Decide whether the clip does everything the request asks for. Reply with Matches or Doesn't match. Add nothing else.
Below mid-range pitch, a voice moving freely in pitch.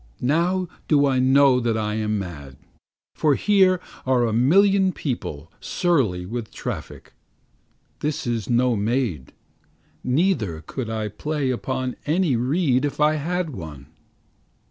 Matches